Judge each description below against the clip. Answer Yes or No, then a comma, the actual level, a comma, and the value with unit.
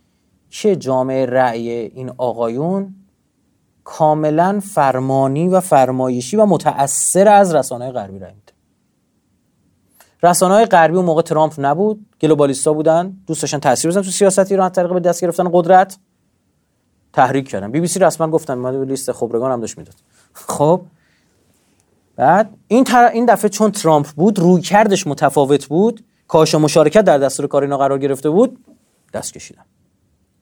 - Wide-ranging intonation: Yes, wide, 6.4 semitones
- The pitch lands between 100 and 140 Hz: No, medium, 155 Hz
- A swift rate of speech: No, average, 145 wpm